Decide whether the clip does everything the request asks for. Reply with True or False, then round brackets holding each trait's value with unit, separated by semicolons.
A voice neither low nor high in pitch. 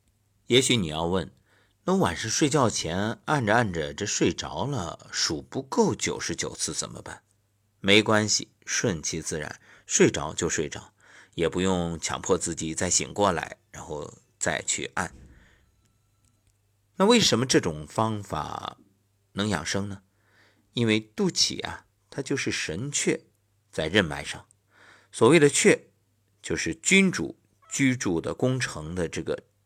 False (100 Hz)